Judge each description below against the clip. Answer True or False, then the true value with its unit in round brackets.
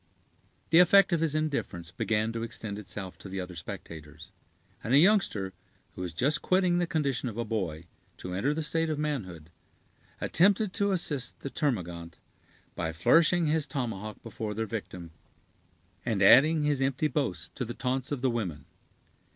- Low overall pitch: True (120 Hz)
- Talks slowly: False (165 wpm)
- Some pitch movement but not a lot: False (8.4 semitones)